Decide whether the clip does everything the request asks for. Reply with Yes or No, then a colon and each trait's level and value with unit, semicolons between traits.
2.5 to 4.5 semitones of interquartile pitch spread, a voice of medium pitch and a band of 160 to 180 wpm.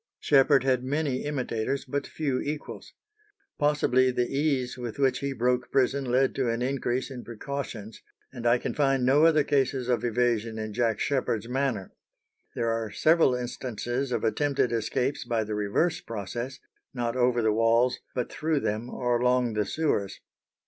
No: average, 2.8 semitones; low, 125 Hz; average, 165 wpm